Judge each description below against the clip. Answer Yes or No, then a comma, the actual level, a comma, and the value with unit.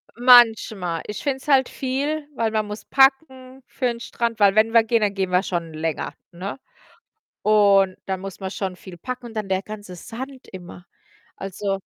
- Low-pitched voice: No, high, 215 Hz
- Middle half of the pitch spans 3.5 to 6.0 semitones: Yes, average, 4.7 semitones